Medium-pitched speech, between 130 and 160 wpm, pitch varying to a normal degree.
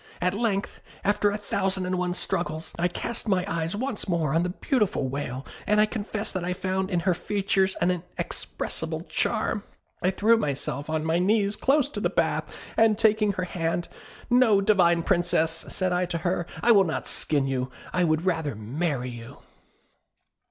No: medium, 180 Hz; average, 180 wpm; average, 3.8 semitones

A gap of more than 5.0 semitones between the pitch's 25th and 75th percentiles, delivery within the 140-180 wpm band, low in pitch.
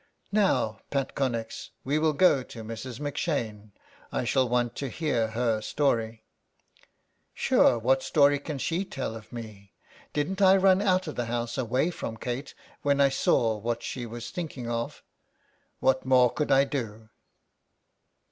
No: average, 4.0 semitones; average, 160 wpm; low, 130 Hz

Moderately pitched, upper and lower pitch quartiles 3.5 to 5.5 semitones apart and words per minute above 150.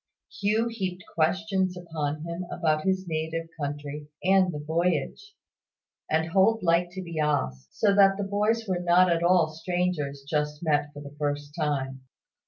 Yes: medium, 170 Hz; average, 3.9 semitones; average, 165 wpm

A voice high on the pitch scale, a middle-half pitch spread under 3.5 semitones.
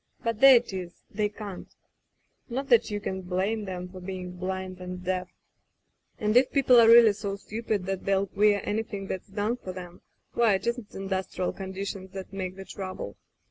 Yes: high, 195 Hz; narrow, 2.6 semitones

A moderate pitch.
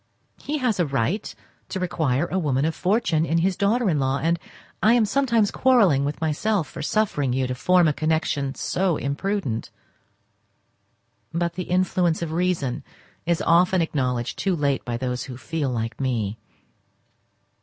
Yes: medium, 165 Hz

